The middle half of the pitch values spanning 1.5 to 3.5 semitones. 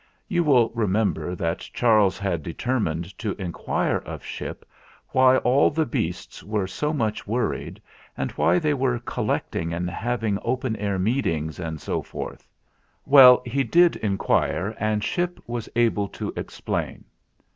No: average, 5.3 semitones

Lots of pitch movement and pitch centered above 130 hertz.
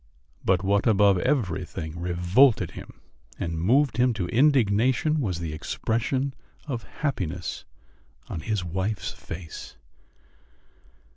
No: wide, 6.1 semitones; low, 100 Hz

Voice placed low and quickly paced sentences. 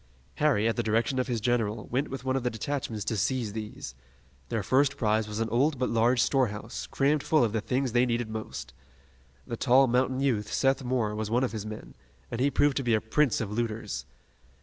Yes: low, 120 Hz; fast, 215 wpm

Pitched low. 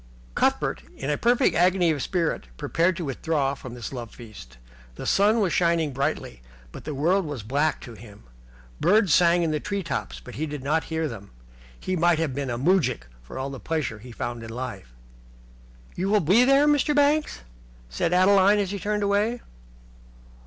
No: medium, 160 Hz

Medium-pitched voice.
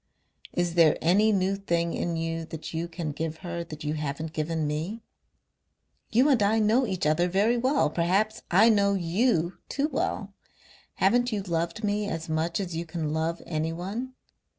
Yes: medium, 175 Hz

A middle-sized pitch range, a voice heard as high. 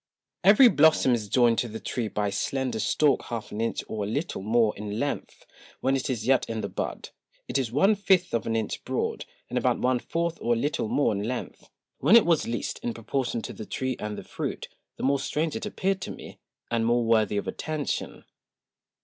No: average, 4.7 semitones; low, 120 Hz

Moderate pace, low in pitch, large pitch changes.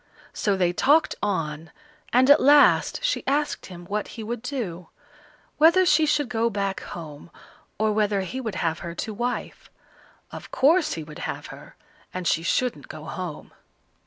No: average, 165 wpm; high, 210 Hz; wide, 7.2 semitones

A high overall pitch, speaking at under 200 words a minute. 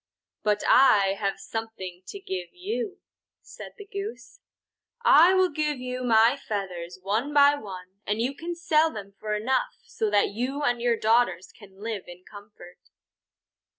Yes: high, 225 Hz; average, 150 wpm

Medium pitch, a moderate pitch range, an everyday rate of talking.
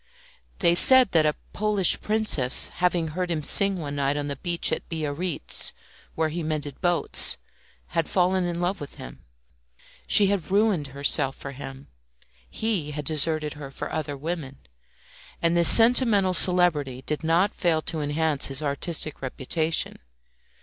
Yes: medium, 160 Hz; average, 3.8 semitones; average, 150 wpm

